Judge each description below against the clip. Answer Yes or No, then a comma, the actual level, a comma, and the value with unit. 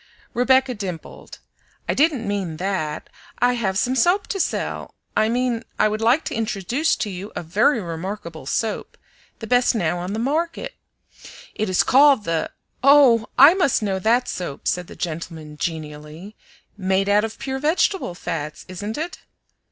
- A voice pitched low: No, high, 215 Hz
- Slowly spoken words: No, average, 160 wpm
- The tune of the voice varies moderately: No, wide, 6.1 semitones